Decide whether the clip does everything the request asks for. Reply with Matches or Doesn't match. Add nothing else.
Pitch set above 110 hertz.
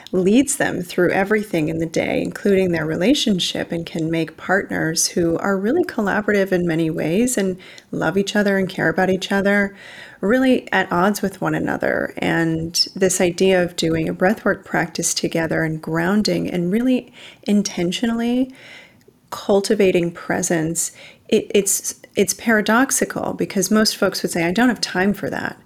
Matches